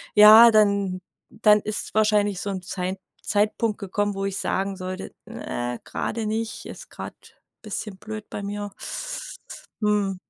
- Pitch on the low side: No, high, 205 Hz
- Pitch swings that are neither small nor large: No, narrow, 1.6 semitones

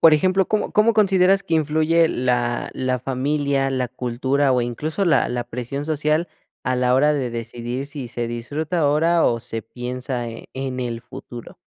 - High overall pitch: No, low, 135 Hz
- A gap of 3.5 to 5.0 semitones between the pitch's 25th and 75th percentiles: Yes, average, 4.2 semitones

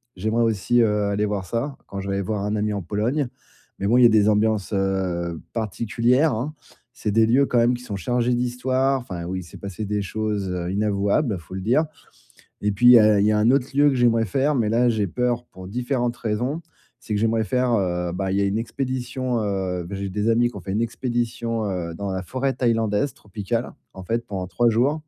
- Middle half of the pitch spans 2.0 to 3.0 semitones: No, average, 3.6 semitones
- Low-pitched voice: Yes, low, 110 Hz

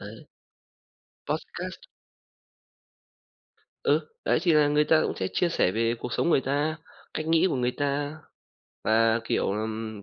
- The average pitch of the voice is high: No, medium, 140 Hz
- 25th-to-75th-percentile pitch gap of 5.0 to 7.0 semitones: Yes, wide, 5.6 semitones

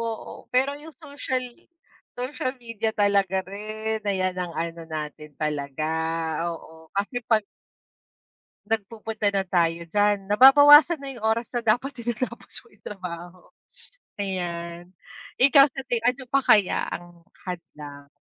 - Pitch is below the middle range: No, high, 205 Hz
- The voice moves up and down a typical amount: No, wide, 6.0 semitones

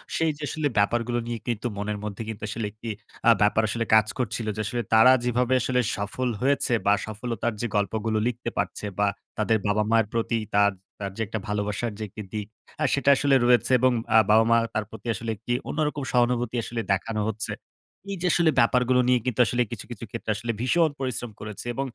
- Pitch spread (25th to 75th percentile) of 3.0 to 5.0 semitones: No, narrow, 2.6 semitones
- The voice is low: Yes, low, 115 Hz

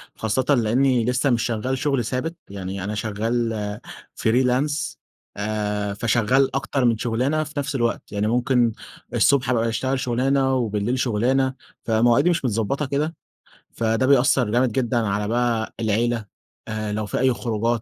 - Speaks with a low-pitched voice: Yes, low, 120 Hz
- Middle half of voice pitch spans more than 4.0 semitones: No, average, 3.2 semitones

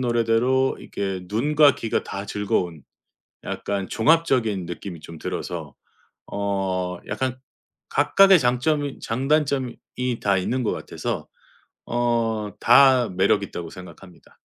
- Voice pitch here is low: Yes, low, 115 Hz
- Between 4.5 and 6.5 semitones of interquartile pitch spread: Yes, average, 5.2 semitones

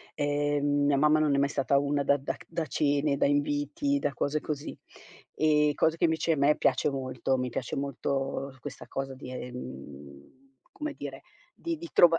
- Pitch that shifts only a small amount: Yes, narrow, 1.9 semitones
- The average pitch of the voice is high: No, medium, 145 Hz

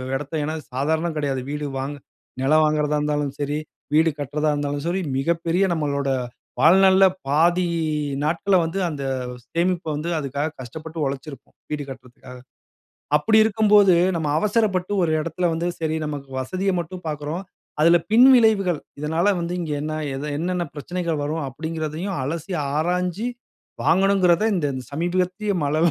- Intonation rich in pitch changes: No, average, 3.5 semitones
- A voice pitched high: No, medium, 160 Hz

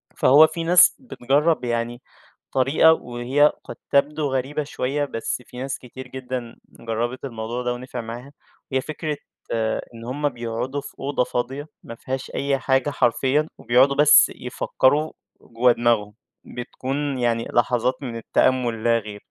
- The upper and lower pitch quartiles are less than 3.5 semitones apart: Yes, average, 3.0 semitones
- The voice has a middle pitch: No, low, 130 Hz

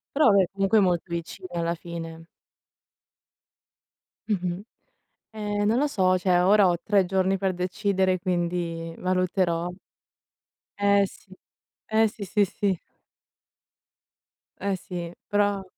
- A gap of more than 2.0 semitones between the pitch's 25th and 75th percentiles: Yes, narrow, 2.4 semitones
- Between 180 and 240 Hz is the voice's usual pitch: Yes, medium, 185 Hz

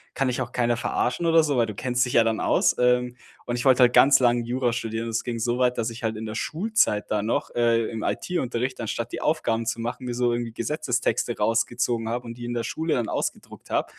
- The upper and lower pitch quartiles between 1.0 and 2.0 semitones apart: Yes, narrow, 1.5 semitones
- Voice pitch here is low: Yes, low, 120 Hz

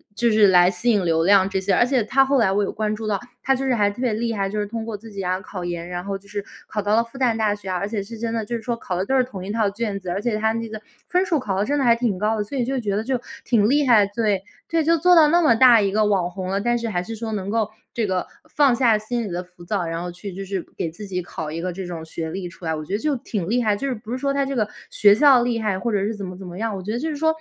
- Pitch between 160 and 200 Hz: No, high, 210 Hz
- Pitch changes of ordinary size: Yes, average, 3.7 semitones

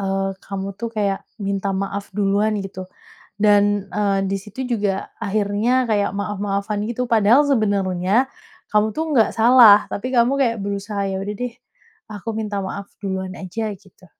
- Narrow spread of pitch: Yes, narrow, 2.1 semitones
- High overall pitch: Yes, high, 205 Hz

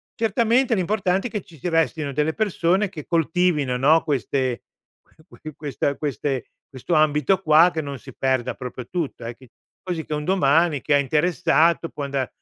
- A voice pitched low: No, medium, 155 Hz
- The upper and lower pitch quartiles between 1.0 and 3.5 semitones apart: No, average, 4.2 semitones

